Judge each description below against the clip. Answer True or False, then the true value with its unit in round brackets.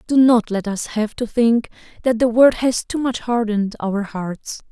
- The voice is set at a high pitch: True (225 Hz)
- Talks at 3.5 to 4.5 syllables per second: True (4.4 syllables/s)